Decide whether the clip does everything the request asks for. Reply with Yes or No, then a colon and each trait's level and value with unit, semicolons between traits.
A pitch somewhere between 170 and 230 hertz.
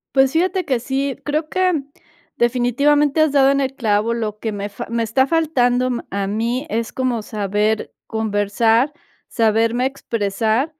No: high, 245 Hz